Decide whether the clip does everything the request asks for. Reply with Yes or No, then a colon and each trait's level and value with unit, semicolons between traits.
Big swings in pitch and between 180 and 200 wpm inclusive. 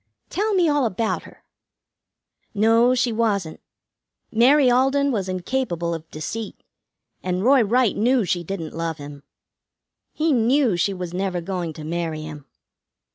No: wide, 6.8 semitones; average, 140 wpm